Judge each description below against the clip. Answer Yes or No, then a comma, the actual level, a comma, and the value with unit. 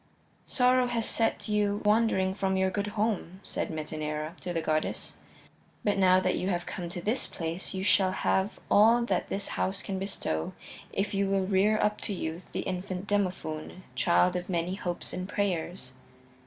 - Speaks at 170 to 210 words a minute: Yes, average, 175 wpm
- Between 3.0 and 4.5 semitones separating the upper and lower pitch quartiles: No, narrow, 2.6 semitones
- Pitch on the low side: No, high, 190 Hz